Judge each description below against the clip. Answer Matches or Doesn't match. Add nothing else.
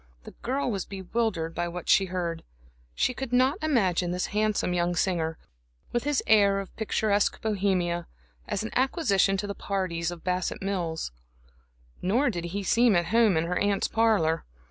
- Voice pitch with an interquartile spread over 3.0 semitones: Matches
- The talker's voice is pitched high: Matches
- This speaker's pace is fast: Doesn't match